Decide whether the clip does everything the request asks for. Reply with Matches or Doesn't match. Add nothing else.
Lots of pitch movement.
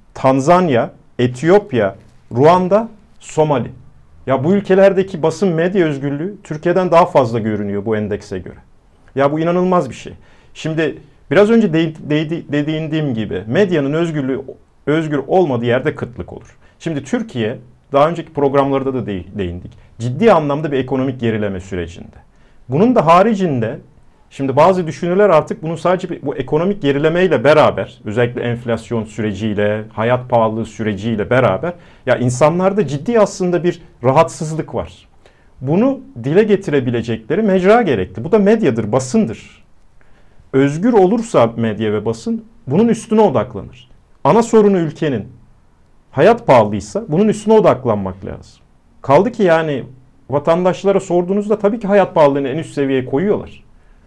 Matches